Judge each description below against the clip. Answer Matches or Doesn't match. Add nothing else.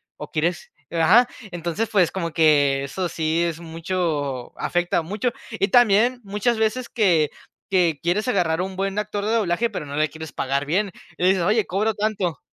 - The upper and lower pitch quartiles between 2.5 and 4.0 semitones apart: Doesn't match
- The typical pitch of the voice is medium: Matches